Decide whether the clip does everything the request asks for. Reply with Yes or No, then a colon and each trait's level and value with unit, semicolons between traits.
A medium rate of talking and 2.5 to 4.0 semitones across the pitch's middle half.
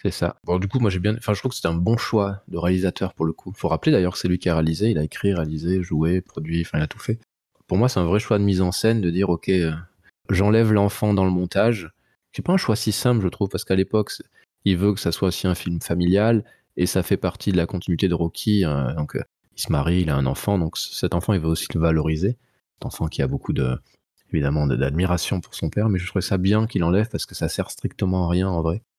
No: fast, 285 wpm; average, 3.3 semitones